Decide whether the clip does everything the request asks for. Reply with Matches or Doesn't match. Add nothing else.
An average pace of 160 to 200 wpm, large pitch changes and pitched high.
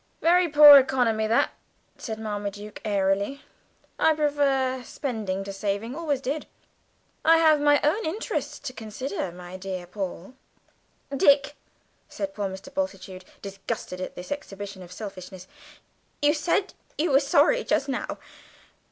Doesn't match